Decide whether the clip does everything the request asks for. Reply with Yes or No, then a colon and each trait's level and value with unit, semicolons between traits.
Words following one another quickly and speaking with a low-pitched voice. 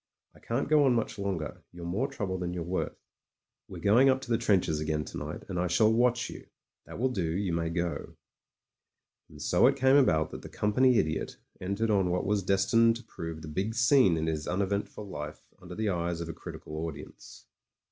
Yes: fast, 210 wpm; very low, 95 Hz